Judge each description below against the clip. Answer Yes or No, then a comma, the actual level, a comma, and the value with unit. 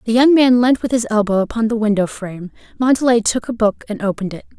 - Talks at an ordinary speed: No, fast, 235 wpm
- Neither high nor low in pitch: No, high, 225 Hz